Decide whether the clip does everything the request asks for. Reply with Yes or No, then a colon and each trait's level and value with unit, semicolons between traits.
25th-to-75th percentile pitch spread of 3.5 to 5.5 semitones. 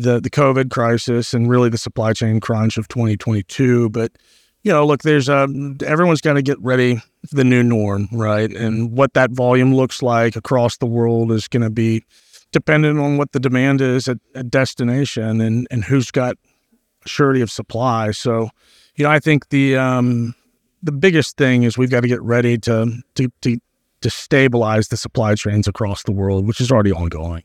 No: average, 3.1 semitones